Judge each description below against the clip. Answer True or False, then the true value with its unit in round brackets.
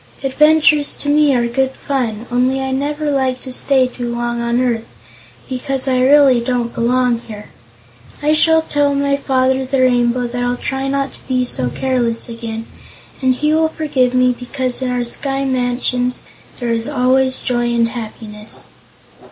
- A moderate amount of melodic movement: False (2.2 semitones)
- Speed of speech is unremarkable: True (170 wpm)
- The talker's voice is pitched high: True (255 Hz)